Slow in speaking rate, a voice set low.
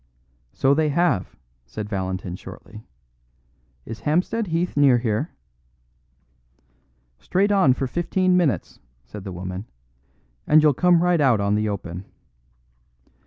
Yes: slow, 120 wpm; low, 130 Hz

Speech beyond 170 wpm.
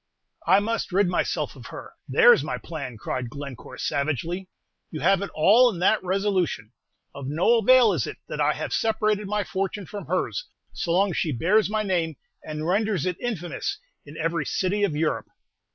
Yes: average, 185 wpm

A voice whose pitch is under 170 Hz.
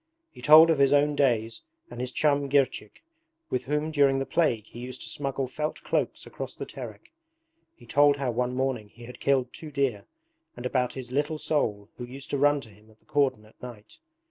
Yes: low, 135 Hz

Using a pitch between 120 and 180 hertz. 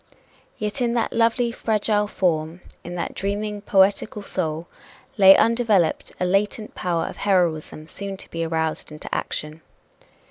No: high, 195 Hz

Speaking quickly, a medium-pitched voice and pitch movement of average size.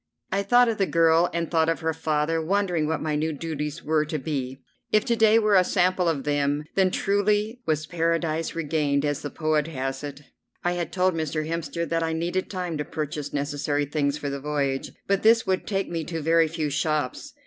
Yes: fast, 210 wpm; medium, 160 Hz; average, 3.1 semitones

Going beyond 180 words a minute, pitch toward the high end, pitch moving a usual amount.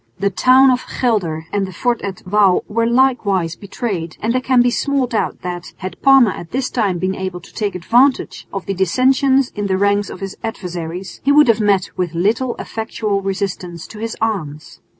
Yes: average, 195 wpm; high, 205 Hz; average, 4.7 semitones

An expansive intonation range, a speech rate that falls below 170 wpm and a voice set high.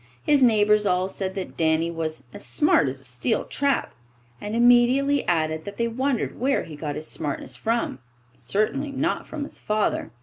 No: wide, 7.7 semitones; average, 175 wpm; high, 205 Hz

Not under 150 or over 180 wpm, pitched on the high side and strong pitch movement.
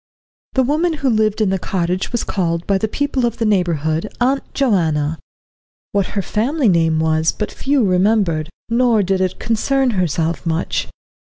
Yes: average, 165 wpm; high, 200 Hz; wide, 6.1 semitones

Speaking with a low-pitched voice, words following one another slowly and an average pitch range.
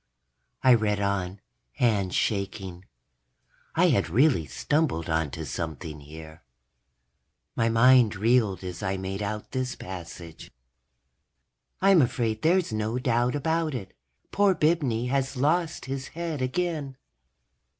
No: low, 115 Hz; slow, 120 wpm; wide, 6.6 semitones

